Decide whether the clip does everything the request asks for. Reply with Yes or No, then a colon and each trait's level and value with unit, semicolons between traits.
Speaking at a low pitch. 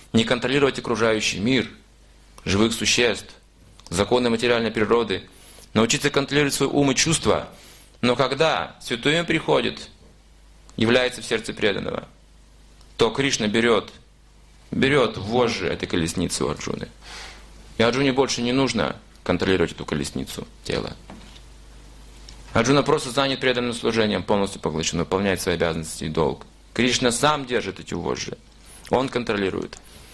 Yes: low, 115 Hz